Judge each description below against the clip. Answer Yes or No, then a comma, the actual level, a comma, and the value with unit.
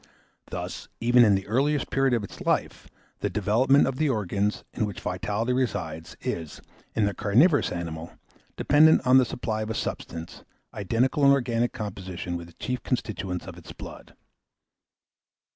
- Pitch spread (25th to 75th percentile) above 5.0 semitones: Yes, wide, 5.4 semitones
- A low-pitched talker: Yes, low, 110 Hz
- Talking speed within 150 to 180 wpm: Yes, average, 160 wpm